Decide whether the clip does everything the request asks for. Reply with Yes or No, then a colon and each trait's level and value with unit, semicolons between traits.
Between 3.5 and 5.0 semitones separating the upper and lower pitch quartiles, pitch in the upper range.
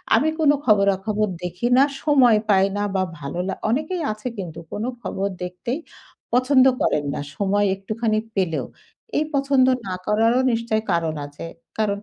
Yes: average, 4.7 semitones; high, 215 Hz